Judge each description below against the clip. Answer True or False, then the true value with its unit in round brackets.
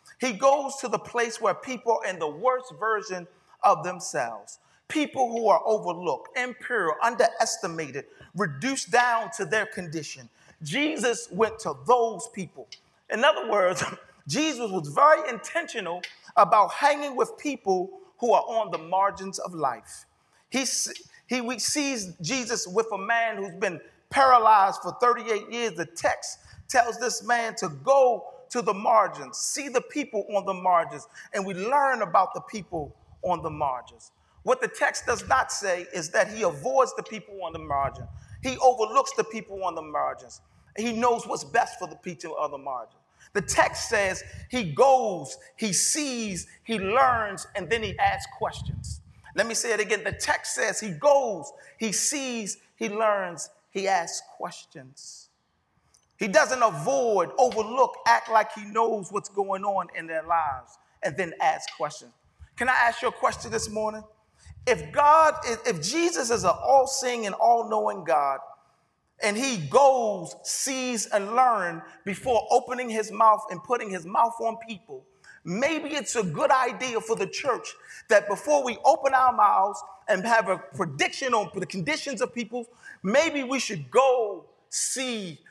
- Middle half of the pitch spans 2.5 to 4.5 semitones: False (4.9 semitones)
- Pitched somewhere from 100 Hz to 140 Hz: False (225 Hz)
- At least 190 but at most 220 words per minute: False (165 wpm)